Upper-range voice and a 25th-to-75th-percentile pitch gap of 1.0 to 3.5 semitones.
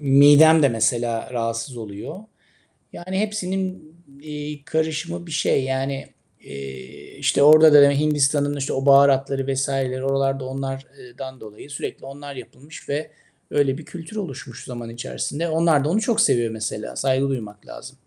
No: medium, 140 Hz; average, 2.9 semitones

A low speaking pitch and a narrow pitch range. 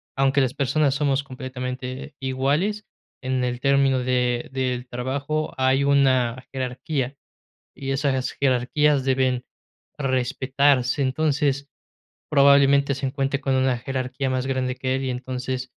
Yes: low, 130 Hz; narrow, 1.5 semitones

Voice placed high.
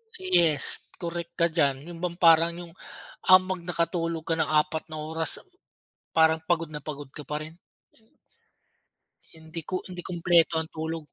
No: medium, 165 Hz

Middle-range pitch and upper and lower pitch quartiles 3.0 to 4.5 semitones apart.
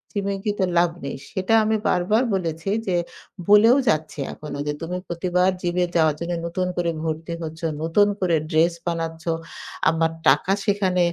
No: medium, 175 Hz; narrow, 2.6 semitones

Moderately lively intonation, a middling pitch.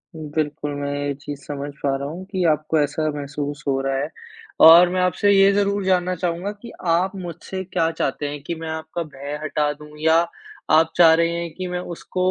Yes: average, 3.5 semitones; medium, 160 Hz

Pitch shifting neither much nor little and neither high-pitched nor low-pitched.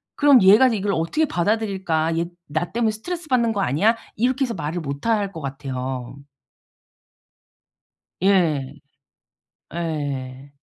No: wide, 7.6 semitones; medium, 175 Hz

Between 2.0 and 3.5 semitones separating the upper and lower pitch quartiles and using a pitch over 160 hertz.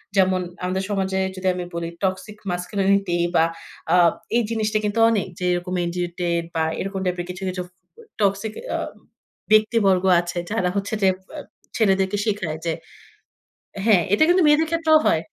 Yes: average, 2.9 semitones; high, 190 Hz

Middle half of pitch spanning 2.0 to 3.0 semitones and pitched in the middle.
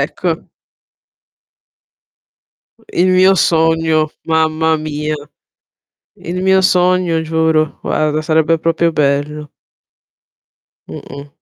No: narrow, 1.6 semitones; medium, 160 Hz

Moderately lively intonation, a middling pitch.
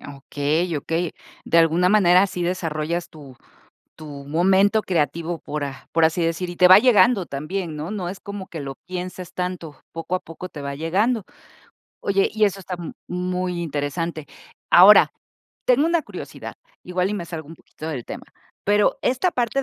Yes: average, 3.4 semitones; medium, 175 Hz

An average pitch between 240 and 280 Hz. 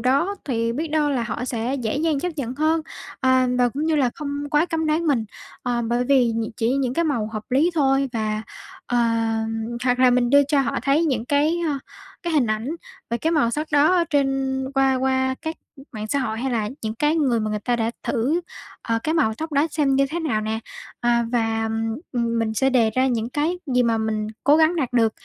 Yes: very high, 260 Hz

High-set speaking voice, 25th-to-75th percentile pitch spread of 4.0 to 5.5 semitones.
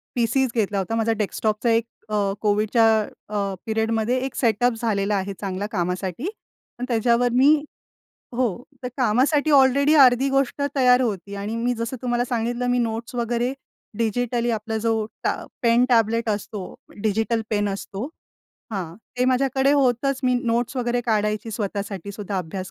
No: high, 230 Hz; average, 3.0 semitones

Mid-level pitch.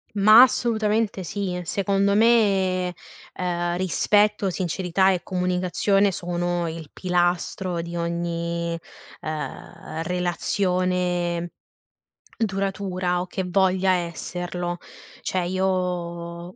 Yes: medium, 180 Hz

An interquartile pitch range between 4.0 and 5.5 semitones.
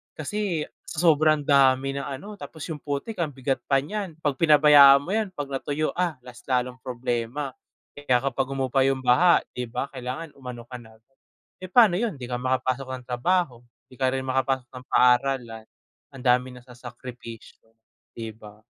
No: average, 3.2 semitones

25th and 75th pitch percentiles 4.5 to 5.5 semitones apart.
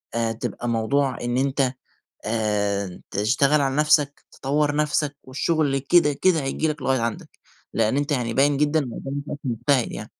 No: average, 3.8 semitones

